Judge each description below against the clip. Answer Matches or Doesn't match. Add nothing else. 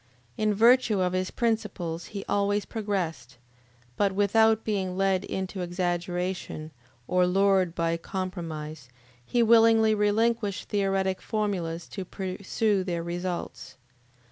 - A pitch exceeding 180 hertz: Matches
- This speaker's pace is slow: Matches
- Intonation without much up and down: Doesn't match